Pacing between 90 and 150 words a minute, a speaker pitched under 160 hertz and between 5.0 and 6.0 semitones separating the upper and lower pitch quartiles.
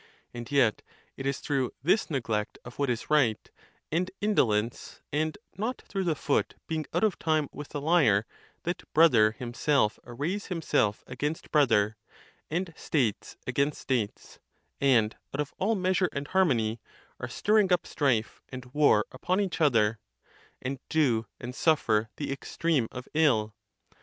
Yes: average, 145 wpm; medium, 140 Hz; wide, 5.6 semitones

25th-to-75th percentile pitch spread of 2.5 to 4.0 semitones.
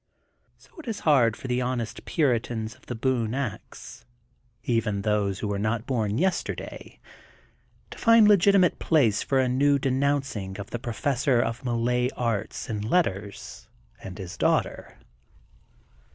No: average, 4.4 semitones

